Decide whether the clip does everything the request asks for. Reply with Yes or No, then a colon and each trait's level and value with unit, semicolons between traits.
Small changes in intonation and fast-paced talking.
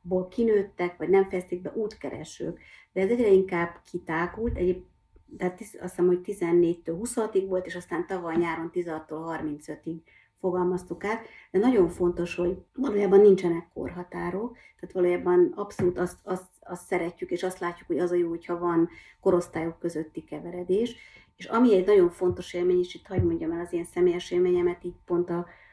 Yes: narrow, 1.3 semitones; fast, 170 wpm